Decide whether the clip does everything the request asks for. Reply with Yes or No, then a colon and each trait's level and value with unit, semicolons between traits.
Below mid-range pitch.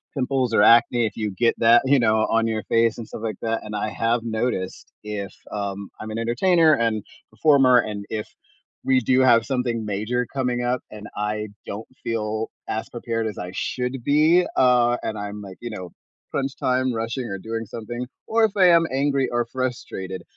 Yes: low, 115 Hz